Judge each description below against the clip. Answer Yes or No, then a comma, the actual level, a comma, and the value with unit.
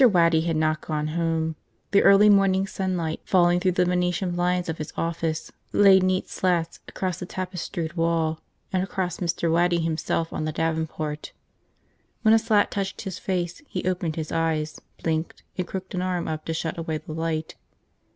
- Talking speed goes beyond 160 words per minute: Yes, average, 175 wpm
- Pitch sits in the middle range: Yes, medium, 170 Hz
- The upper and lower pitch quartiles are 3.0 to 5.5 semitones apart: No, narrow, 2.4 semitones